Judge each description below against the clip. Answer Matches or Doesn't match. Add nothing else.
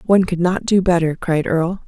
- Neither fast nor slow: Doesn't match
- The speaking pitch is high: Doesn't match